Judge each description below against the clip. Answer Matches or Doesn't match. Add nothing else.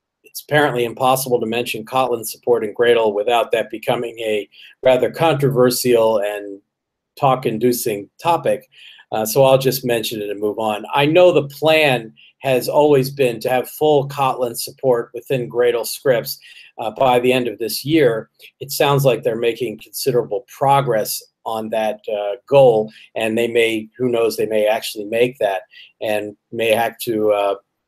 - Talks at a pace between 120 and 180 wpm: Matches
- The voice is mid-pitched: Doesn't match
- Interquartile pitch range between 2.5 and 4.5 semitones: Doesn't match